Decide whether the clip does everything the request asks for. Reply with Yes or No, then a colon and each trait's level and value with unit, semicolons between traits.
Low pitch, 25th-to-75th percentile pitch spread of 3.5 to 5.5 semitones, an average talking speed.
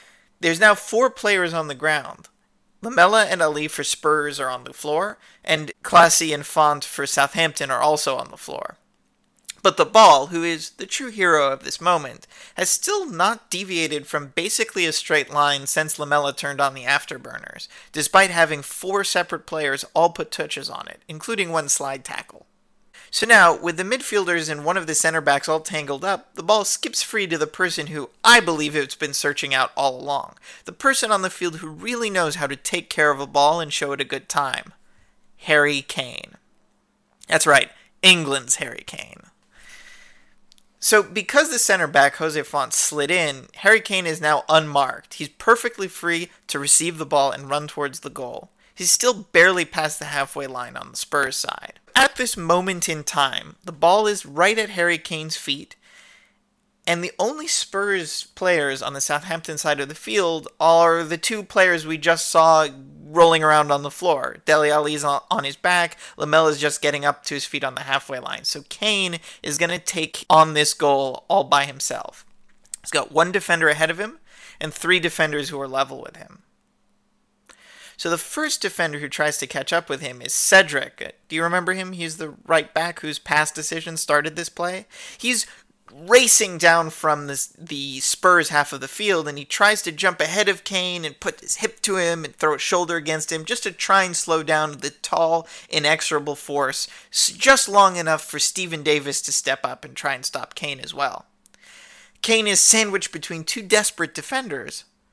No: medium, 165 Hz; average, 4.1 semitones; average, 190 wpm